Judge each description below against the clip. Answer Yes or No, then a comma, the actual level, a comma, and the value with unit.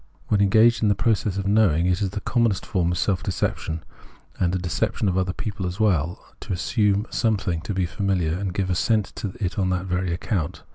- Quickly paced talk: Yes, fast, 210 wpm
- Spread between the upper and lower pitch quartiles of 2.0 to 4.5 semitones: Yes, narrow, 2.6 semitones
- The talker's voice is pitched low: Yes, very low, 95 Hz